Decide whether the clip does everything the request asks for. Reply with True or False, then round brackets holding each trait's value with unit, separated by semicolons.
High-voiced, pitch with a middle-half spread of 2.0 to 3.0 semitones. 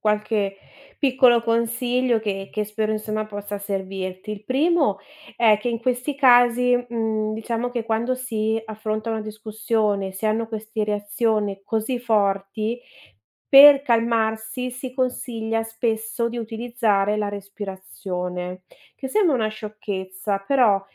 True (220 Hz; 2.5 semitones)